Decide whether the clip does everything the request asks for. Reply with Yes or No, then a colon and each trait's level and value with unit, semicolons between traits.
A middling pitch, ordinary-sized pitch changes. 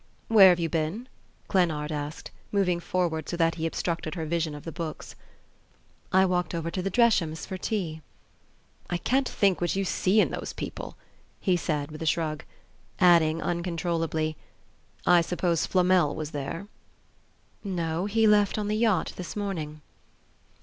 Yes: medium, 175 Hz; average, 3.0 semitones